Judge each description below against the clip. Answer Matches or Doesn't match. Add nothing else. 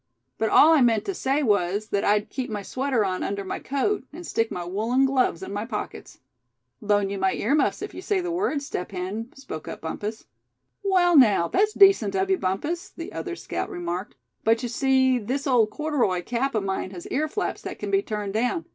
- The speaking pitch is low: Doesn't match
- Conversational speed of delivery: Doesn't match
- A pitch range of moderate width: Doesn't match